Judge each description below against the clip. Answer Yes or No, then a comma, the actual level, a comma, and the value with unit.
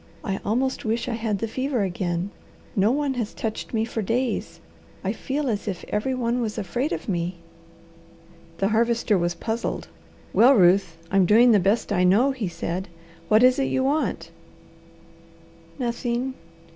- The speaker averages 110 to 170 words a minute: Yes, average, 160 wpm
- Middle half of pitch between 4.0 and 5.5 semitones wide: Yes, average, 4.3 semitones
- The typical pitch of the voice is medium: No, high, 225 Hz